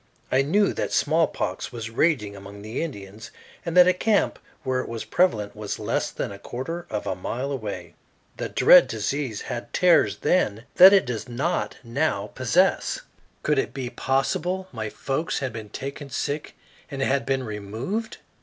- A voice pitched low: Yes, low, 130 Hz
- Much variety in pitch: Yes, wide, 6.7 semitones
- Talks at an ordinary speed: Yes, average, 170 wpm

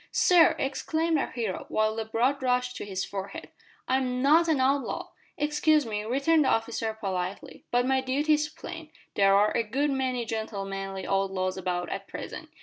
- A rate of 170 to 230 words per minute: Yes, average, 175 wpm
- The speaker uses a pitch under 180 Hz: No, high, 245 Hz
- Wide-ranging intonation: Yes, wide, 6.0 semitones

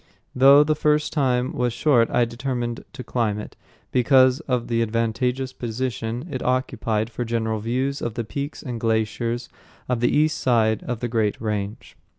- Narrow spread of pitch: Yes, narrow, 2.2 semitones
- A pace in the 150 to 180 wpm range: Yes, average, 160 wpm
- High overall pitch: No, low, 120 Hz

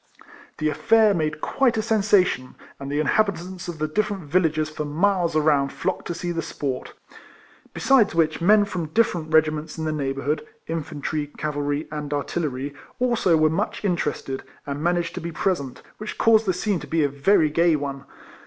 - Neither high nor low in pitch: Yes, medium, 160 Hz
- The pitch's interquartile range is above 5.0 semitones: No, average, 4.0 semitones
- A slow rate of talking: No, average, 175 wpm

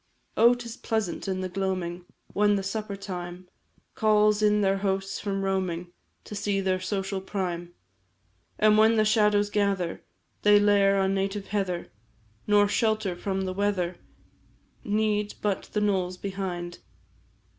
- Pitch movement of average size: No, narrow, 1.9 semitones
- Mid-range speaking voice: No, high, 195 Hz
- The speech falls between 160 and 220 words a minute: No, average, 140 wpm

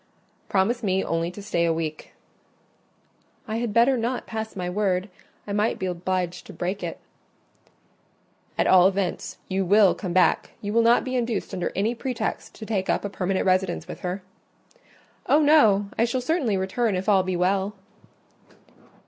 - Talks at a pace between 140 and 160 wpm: No, average, 170 wpm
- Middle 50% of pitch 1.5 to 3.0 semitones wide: No, average, 3.6 semitones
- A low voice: No, high, 195 Hz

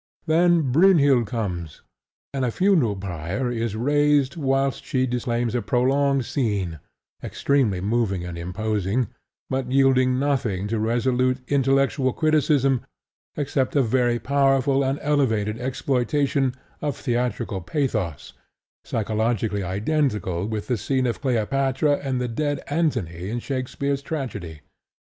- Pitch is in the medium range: No, low, 125 Hz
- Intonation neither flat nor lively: Yes, average, 4.2 semitones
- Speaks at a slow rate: Yes, slow, 120 wpm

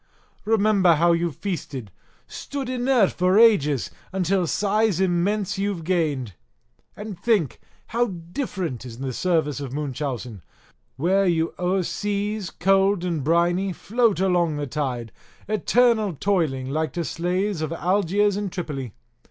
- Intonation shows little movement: No, average, 4.9 semitones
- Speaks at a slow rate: Yes, slow, 125 wpm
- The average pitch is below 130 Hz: No, medium, 180 Hz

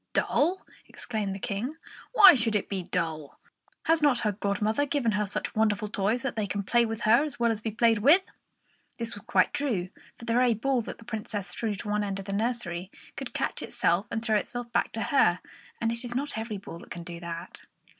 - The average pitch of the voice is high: Yes, high, 220 Hz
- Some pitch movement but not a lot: Yes, average, 3.2 semitones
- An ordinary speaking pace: No, fast, 225 wpm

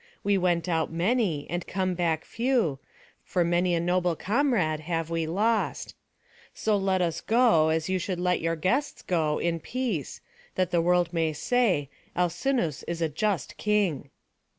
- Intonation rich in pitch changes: No, average, 3.6 semitones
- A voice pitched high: No, medium, 175 Hz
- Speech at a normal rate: Yes, average, 160 wpm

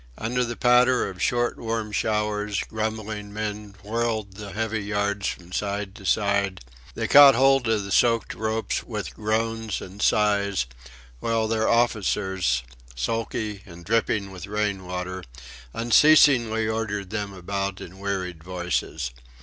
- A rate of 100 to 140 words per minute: Yes, slow, 135 wpm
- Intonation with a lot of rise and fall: No, narrow, 2.4 semitones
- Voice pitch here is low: Yes, low, 105 Hz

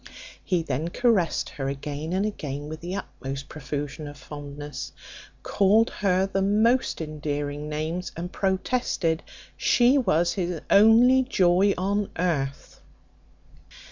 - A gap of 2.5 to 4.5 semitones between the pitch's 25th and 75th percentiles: No, average, 5.2 semitones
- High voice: No, medium, 170 Hz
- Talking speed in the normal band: No, slow, 125 wpm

